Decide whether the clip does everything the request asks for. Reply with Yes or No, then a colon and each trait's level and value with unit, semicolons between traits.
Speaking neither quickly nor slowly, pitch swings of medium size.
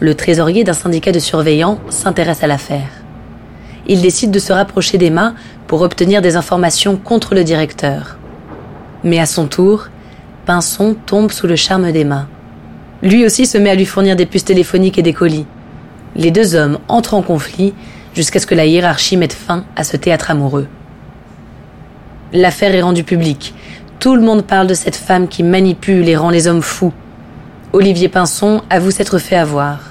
Yes: average, 175 wpm; average, 3.3 semitones